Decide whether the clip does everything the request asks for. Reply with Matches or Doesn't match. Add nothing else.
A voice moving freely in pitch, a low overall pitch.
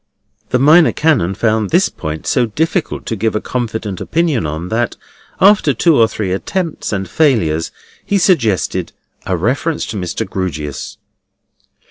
Matches